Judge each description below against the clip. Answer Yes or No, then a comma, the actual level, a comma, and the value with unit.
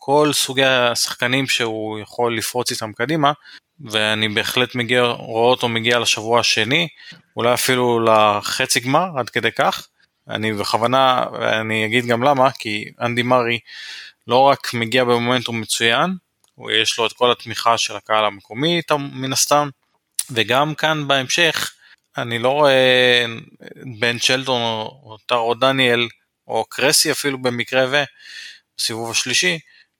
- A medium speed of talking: Yes, average, 130 wpm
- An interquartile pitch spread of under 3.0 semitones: Yes, narrow, 2.6 semitones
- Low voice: Yes, low, 125 Hz